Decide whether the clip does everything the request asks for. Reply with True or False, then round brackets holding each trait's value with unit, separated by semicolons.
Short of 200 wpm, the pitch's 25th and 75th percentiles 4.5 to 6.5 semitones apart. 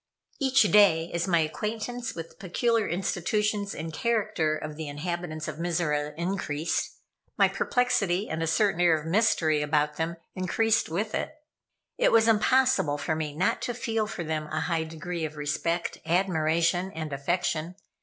True (160 wpm; 5.0 semitones)